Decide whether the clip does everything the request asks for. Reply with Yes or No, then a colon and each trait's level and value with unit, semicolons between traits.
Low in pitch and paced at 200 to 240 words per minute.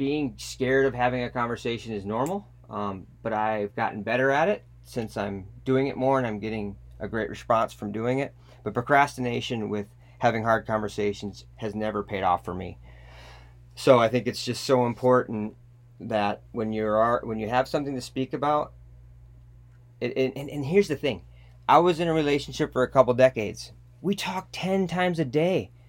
No: low, 120 Hz; average, 185 wpm